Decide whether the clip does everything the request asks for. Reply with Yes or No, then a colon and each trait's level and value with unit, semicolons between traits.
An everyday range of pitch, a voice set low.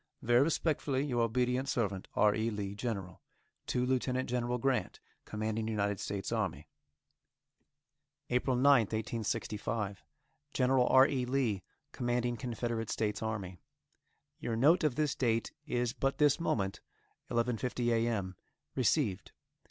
Yes: average, 3.1 semitones; low, 120 Hz